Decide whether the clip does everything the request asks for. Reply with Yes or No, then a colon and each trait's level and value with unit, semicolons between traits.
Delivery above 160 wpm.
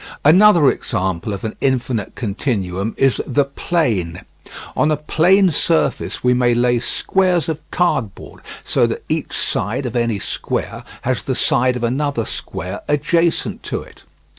No: average, 145 wpm